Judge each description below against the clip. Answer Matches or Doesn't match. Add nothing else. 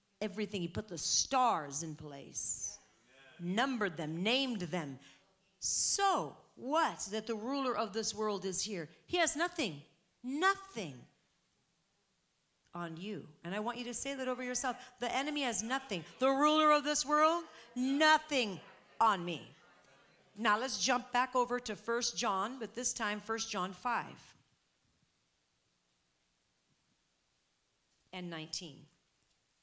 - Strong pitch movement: Matches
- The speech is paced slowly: Matches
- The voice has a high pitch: Matches